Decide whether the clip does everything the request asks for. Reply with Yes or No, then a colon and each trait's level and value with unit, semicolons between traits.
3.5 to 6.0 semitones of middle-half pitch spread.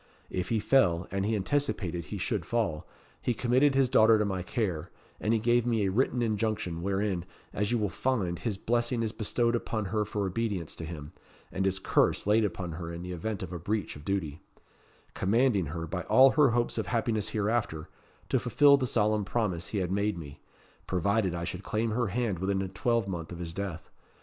Yes: average, 4.4 semitones